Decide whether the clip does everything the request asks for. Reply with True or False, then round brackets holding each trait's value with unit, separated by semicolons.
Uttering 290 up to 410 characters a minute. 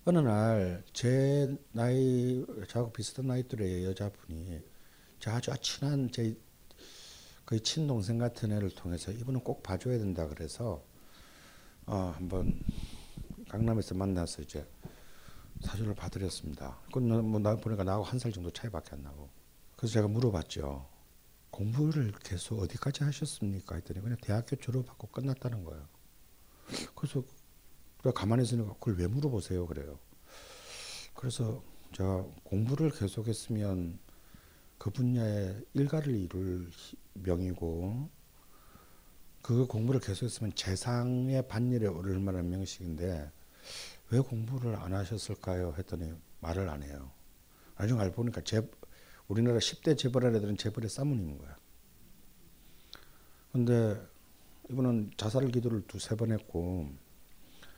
False (275 characters per minute)